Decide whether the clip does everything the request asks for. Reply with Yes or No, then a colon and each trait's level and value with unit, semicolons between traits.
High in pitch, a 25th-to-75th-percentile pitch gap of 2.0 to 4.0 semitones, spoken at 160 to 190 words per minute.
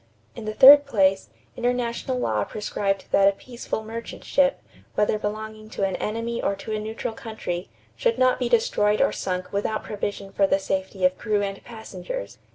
Yes: high, 215 Hz; average, 3.1 semitones; average, 175 wpm